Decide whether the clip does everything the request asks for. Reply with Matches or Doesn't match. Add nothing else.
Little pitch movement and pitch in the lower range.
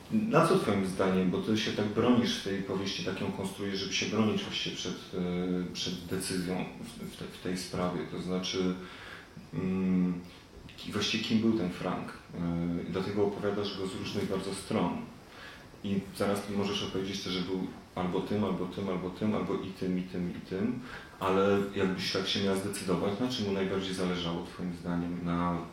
Matches